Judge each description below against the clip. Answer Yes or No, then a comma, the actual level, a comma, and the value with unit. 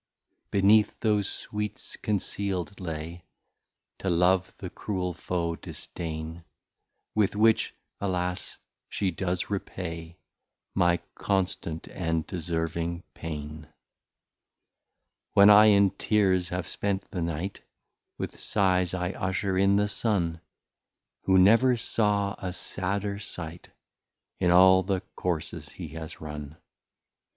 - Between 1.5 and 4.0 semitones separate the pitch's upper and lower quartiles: Yes, average, 2.9 semitones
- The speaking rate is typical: No, slow, 110 wpm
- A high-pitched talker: No, very low, 90 Hz